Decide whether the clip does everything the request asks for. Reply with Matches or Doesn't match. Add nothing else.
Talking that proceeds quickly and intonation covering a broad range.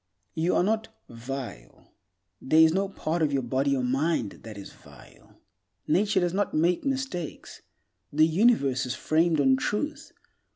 Doesn't match